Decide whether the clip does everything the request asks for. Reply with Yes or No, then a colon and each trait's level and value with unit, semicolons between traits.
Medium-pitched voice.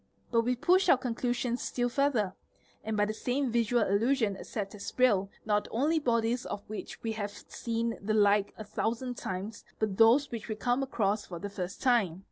No: high, 225 Hz